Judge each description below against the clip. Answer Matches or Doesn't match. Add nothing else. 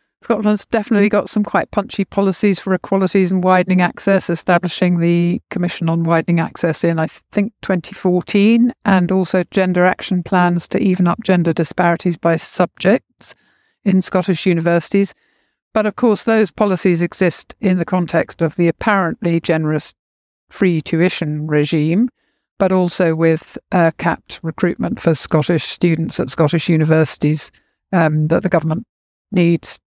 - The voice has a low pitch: Doesn't match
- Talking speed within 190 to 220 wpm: Doesn't match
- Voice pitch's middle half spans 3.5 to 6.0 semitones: Doesn't match